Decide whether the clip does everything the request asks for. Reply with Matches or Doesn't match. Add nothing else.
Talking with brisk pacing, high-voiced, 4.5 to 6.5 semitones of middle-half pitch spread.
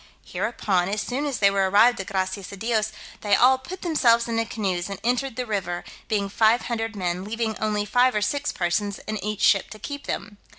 Doesn't match